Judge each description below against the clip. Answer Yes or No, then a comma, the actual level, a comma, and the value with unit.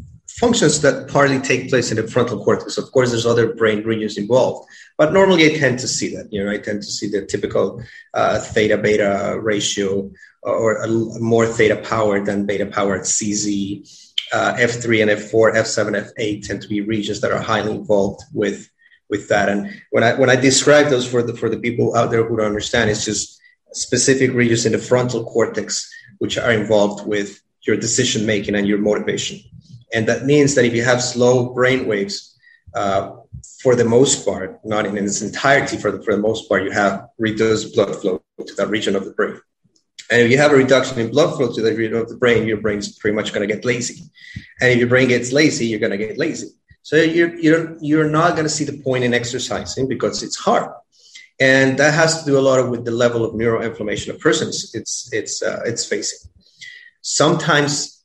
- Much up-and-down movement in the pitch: No, average, 4.3 semitones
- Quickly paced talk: Yes, fast, 210 wpm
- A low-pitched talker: Yes, low, 120 Hz